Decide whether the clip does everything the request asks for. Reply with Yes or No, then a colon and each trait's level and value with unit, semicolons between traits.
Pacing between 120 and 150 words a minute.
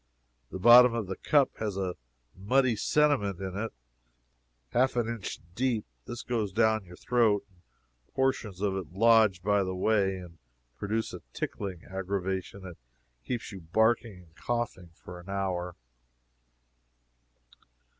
Yes: average, 140 wpm